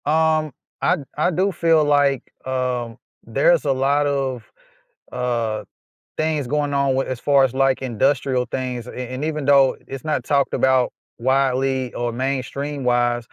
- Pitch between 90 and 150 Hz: Yes, low, 135 Hz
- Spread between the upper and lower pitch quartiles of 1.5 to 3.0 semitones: Yes, narrow, 2.4 semitones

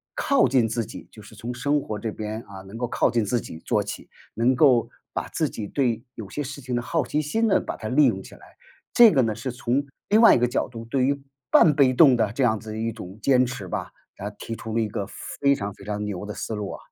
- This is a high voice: No, low, 120 Hz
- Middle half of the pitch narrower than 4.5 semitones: Yes, average, 4.0 semitones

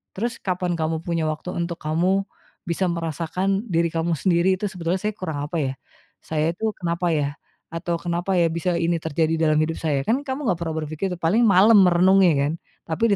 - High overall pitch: No, medium, 170 Hz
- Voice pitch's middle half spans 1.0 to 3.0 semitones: Yes, average, 2.7 semitones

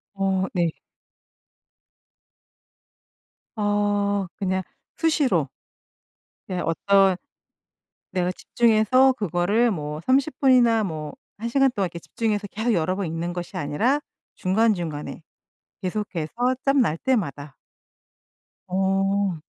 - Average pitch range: Yes, average, 4.5 semitones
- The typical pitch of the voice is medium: No, high, 195 Hz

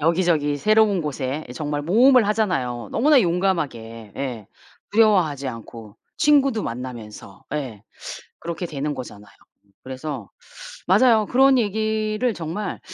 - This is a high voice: No, medium, 160 Hz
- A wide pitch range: Yes, wide, 8.8 semitones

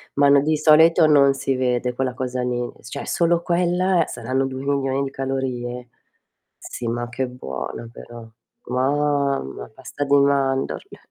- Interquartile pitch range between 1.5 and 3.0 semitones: Yes, narrow, 2.4 semitones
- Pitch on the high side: No, low, 135 Hz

